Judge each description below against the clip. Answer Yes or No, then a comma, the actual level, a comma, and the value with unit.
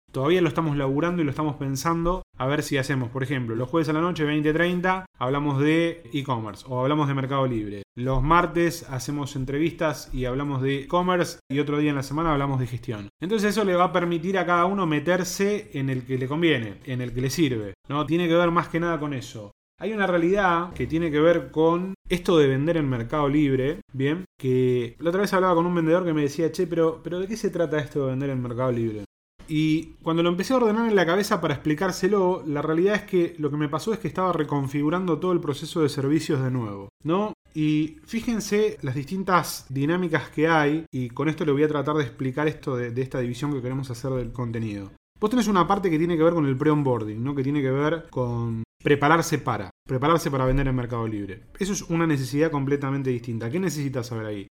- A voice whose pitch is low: No, medium, 150 Hz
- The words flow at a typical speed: No, fast, 225 wpm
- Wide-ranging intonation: No, average, 4.4 semitones